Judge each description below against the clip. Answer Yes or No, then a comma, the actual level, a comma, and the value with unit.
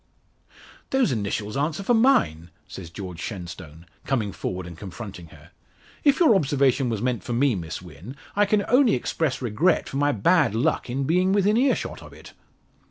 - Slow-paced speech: No, average, 170 wpm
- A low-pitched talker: Yes, low, 130 Hz